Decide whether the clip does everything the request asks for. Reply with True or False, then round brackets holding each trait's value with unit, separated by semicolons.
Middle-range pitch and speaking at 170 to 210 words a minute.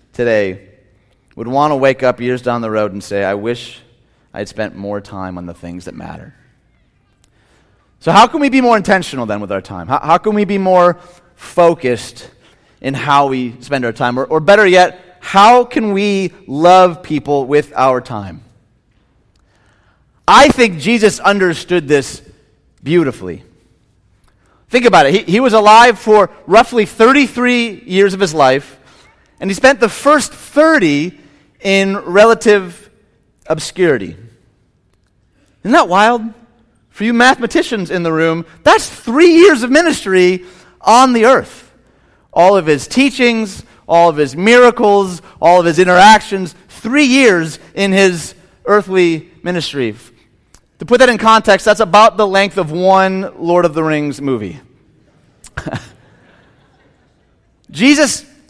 False (175 Hz; 145 wpm)